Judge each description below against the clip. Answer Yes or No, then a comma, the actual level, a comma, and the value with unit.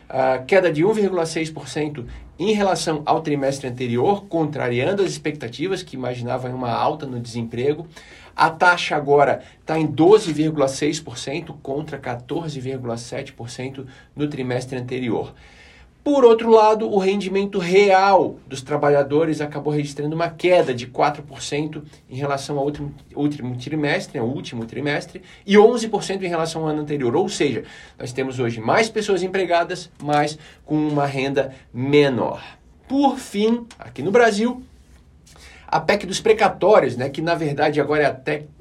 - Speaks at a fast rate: No, average, 130 wpm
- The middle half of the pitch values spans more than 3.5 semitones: Yes, average, 5.3 semitones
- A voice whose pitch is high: No, medium, 150 Hz